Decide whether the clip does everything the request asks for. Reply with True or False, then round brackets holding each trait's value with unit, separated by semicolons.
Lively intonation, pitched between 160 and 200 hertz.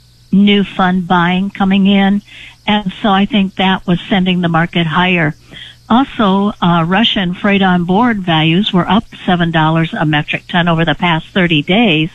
False (2.8 semitones; 185 Hz)